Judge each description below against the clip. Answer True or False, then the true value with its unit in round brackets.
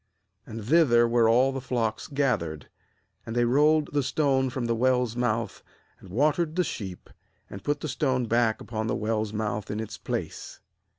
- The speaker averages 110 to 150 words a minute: False (185 wpm)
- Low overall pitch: True (120 Hz)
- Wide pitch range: False (3.5 semitones)